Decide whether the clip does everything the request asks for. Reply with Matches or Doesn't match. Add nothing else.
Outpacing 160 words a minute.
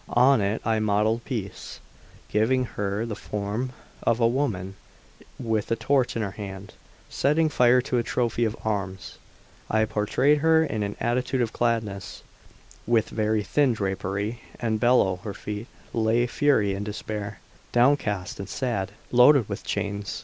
Doesn't match